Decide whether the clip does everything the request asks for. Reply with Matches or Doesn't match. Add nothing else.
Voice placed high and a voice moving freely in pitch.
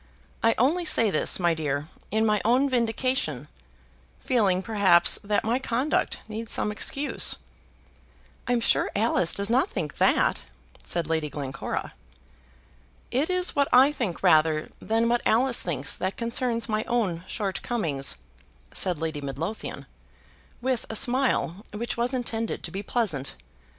Matches